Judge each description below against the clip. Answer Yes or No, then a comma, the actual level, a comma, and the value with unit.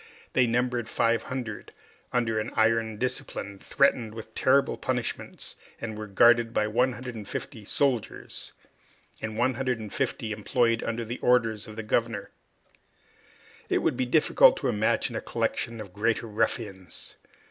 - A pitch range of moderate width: No, narrow, 2.2 semitones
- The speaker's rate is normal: No, slow, 125 wpm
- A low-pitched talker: Yes, low, 115 Hz